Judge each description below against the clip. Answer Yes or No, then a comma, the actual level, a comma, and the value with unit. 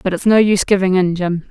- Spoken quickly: Yes, fast, 280 wpm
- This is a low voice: No, medium, 185 Hz